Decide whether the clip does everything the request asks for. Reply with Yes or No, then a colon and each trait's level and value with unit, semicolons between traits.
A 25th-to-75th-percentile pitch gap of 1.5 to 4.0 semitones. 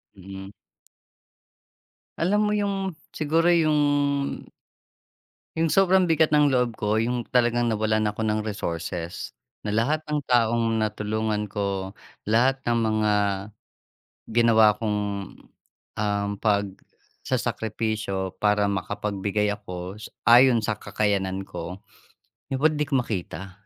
Yes: average, 3.6 semitones